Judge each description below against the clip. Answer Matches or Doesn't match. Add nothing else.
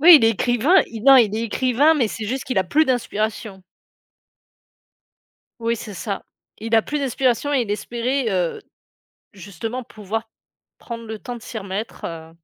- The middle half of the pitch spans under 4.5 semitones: Matches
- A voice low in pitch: Doesn't match